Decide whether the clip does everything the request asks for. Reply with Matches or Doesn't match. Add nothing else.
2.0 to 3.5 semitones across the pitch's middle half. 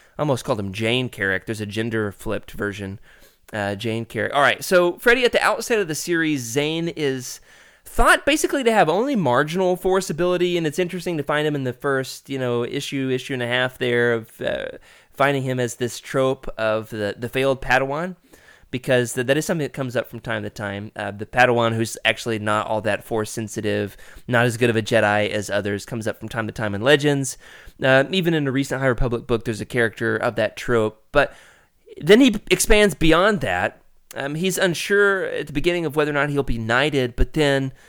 Doesn't match